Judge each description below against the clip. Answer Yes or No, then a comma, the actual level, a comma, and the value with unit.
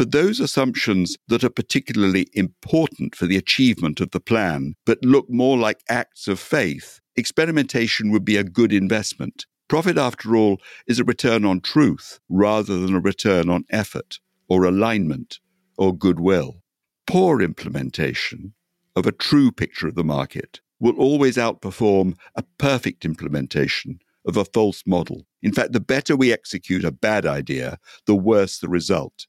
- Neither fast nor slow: Yes, average, 155 wpm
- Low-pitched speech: Yes, low, 100 Hz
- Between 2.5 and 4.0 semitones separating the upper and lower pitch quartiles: No, average, 4.7 semitones